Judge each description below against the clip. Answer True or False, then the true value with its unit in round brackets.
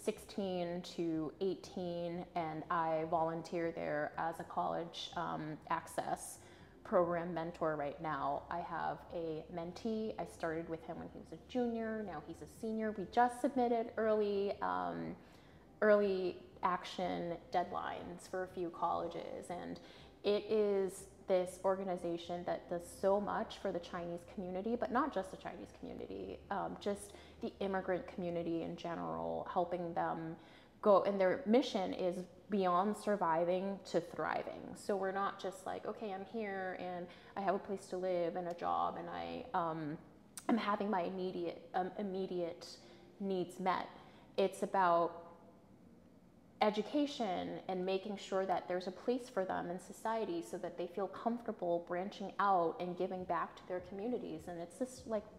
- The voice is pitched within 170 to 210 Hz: True (185 Hz)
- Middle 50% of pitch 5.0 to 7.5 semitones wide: False (3.0 semitones)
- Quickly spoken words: False (155 wpm)